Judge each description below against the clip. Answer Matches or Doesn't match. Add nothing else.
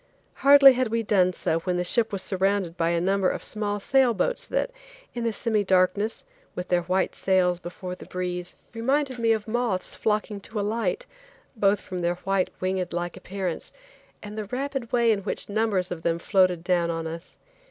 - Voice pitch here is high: Matches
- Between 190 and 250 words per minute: Matches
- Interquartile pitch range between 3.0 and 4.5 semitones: Matches